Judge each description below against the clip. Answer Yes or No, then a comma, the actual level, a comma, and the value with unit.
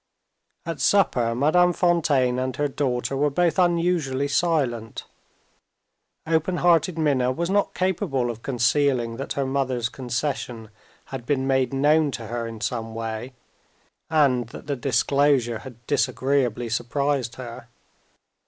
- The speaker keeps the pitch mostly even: No, average, 4.0 semitones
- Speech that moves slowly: Yes, slow, 130 wpm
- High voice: No, low, 135 Hz